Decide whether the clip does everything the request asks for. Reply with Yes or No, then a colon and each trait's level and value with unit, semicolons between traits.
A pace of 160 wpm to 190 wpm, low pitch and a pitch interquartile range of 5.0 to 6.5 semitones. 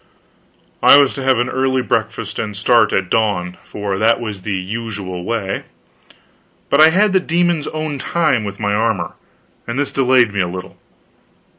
Yes: average, 170 wpm; low, 115 Hz; average, 5.3 semitones